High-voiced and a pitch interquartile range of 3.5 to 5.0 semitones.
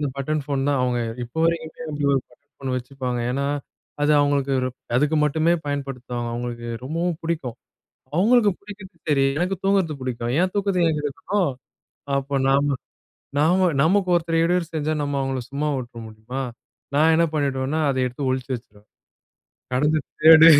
No: medium, 145 Hz; average, 3.9 semitones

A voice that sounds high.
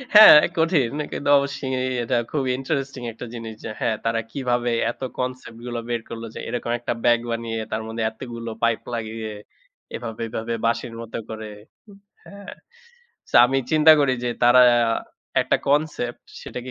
No: low, 120 Hz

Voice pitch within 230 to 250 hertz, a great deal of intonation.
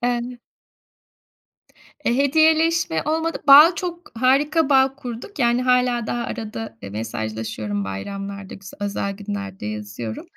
Yes: high, 235 Hz; wide, 6.8 semitones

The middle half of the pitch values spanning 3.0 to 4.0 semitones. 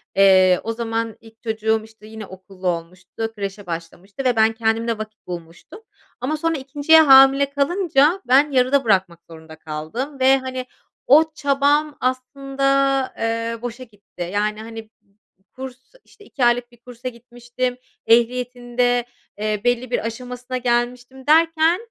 Yes: average, 3.7 semitones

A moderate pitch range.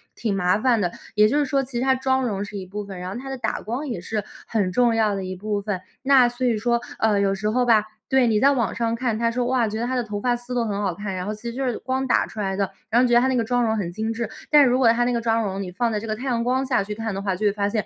Yes: average, 3.3 semitones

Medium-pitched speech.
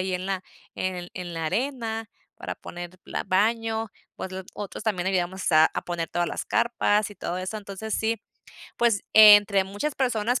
No: high, 200 Hz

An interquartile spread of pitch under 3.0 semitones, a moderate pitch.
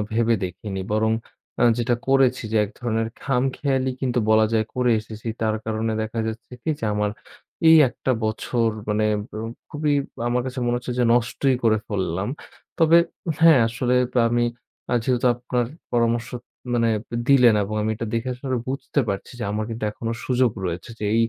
No: narrow, 2.5 semitones; low, 120 Hz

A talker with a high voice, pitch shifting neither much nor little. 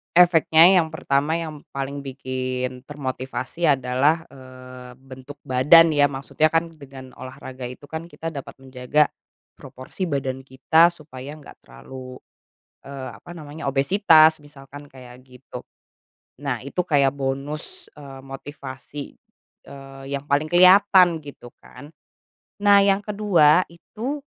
No: medium, 140 Hz; average, 3.6 semitones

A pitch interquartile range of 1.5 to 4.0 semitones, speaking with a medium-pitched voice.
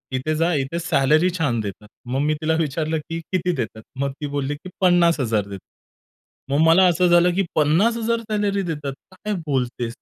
No: average, 4.7 semitones; medium, 155 Hz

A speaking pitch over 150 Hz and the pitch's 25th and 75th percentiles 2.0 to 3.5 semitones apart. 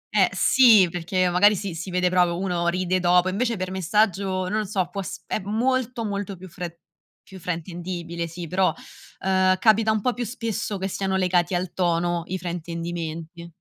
Yes: medium, 185 Hz; narrow, 2.4 semitones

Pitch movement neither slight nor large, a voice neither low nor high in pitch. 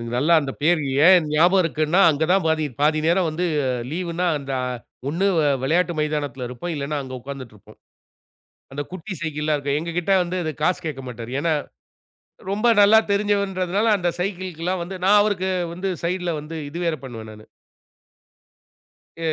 Yes: average, 3.8 semitones; medium, 165 Hz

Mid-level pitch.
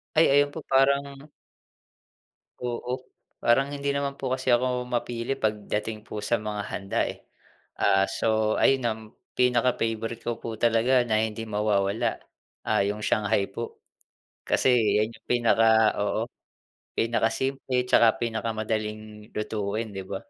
No: low, 115 Hz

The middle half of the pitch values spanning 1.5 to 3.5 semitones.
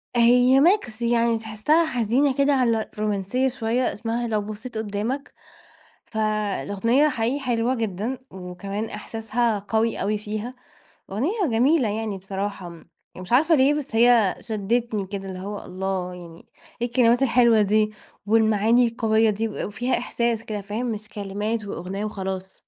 Yes: average, 3.0 semitones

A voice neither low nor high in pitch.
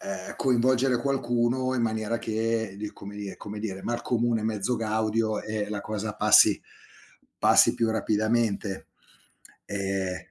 No: low, 110 Hz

